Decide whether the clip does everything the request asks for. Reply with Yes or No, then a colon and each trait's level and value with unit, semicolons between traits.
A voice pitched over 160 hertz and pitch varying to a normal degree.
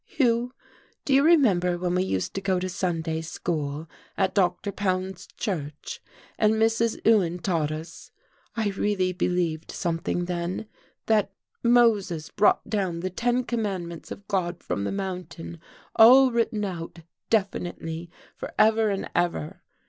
Yes: medium, 185 Hz; average, 4.0 semitones